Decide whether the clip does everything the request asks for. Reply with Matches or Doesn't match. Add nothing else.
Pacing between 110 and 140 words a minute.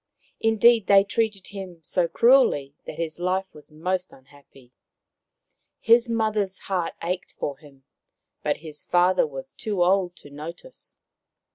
Matches